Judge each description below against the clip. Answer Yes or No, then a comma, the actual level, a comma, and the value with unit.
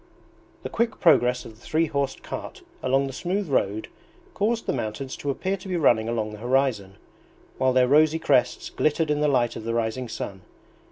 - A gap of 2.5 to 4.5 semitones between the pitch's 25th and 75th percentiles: No, average, 5.0 semitones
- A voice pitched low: Yes, low, 130 Hz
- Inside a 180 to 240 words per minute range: Yes, average, 190 wpm